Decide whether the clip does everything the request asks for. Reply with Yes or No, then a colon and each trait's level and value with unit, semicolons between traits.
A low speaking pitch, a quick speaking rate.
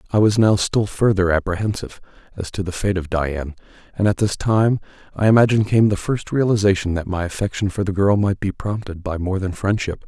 Yes: low, 100 Hz; fast, 210 wpm